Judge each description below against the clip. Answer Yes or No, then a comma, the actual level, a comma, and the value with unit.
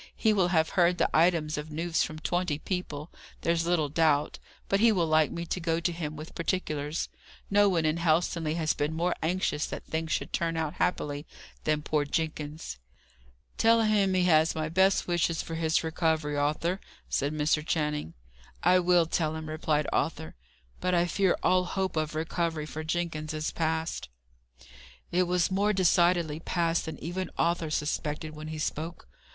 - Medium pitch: Yes, medium, 165 Hz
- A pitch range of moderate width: No, narrow, 2.2 semitones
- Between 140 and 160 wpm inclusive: No, average, 175 wpm